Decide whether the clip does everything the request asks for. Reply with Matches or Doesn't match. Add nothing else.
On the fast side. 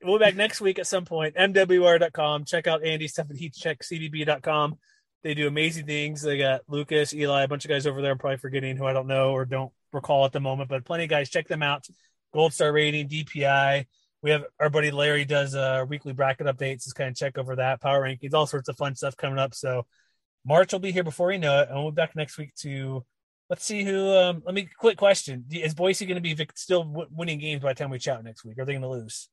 Matches